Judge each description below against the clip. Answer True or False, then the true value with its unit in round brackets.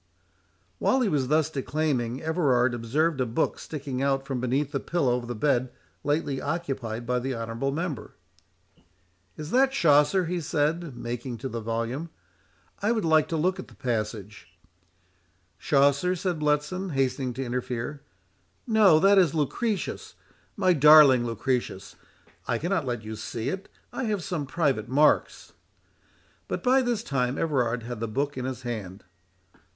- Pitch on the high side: False (140 Hz)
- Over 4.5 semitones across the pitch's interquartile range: True (5.1 semitones)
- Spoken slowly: False (155 wpm)